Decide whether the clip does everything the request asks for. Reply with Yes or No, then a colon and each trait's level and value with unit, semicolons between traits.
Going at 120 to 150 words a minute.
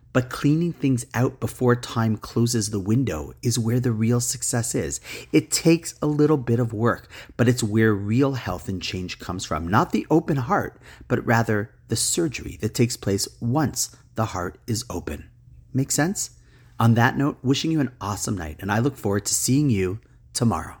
No: average, 185 wpm